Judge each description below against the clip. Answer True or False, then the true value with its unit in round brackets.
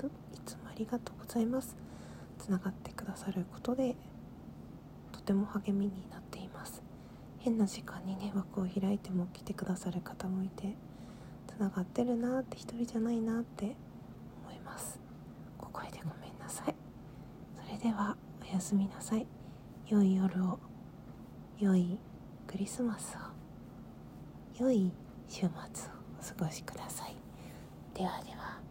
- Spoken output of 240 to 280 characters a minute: True (250 characters per minute)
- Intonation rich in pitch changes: False (3.3 semitones)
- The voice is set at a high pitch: True (200 Hz)